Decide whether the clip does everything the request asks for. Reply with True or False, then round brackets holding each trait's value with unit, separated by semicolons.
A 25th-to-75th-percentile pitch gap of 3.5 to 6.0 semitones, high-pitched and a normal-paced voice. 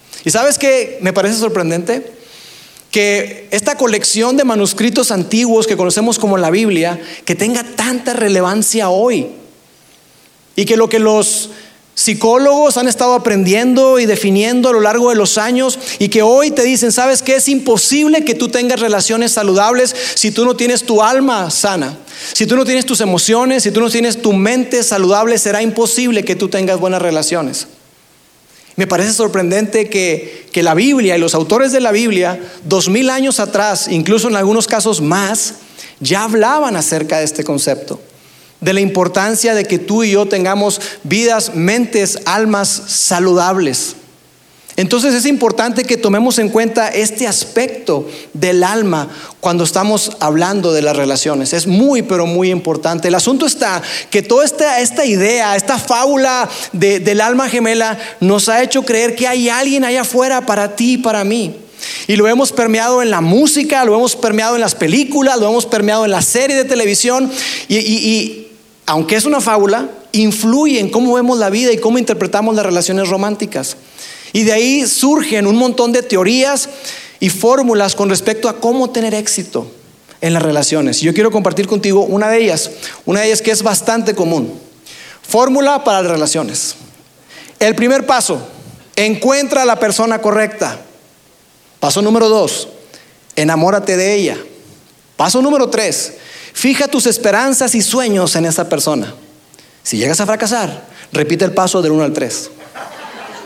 True (4.0 semitones; 220 Hz; 165 wpm)